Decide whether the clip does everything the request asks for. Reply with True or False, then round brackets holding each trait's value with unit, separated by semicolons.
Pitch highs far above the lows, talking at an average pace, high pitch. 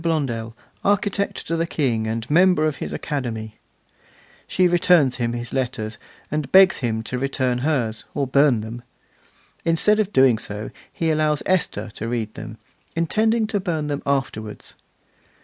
False (6.4 semitones; 150 wpm; 140 Hz)